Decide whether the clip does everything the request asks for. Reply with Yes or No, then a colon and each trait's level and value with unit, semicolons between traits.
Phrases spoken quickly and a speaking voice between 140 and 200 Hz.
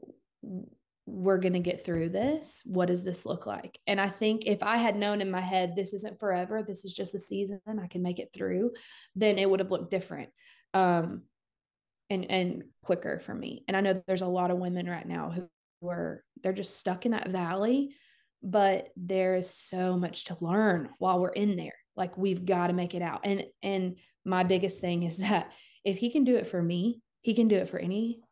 Yes: fast, 220 wpm; high, 190 Hz